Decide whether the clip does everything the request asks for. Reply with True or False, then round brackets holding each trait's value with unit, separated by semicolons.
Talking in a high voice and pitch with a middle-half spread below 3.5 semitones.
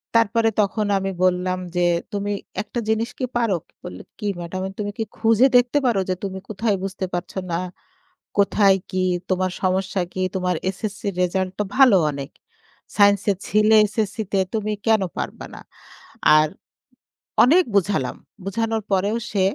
True (200 Hz; 2.9 semitones)